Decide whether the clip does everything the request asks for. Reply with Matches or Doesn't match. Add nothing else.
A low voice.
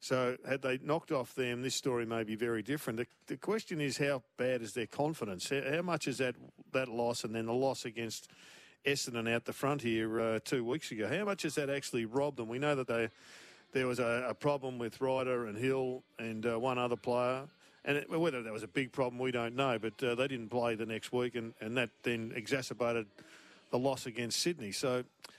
Matches